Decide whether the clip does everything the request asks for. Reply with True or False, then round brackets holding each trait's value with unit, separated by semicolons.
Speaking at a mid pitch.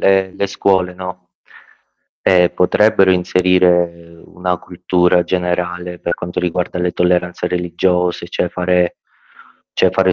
False (90 Hz)